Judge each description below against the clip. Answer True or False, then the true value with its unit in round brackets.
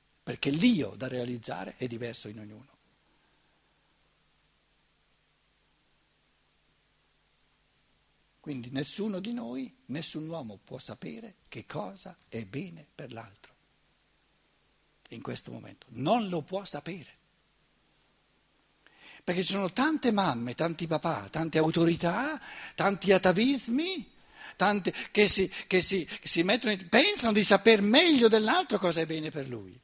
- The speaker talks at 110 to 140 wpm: True (115 wpm)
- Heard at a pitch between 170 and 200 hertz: True (185 Hz)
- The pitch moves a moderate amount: False (6.0 semitones)